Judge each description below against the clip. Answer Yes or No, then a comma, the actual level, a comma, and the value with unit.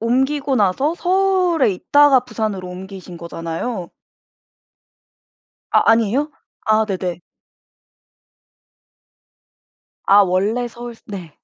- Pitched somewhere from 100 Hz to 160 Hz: No, high, 220 Hz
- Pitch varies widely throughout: Yes, wide, 6.3 semitones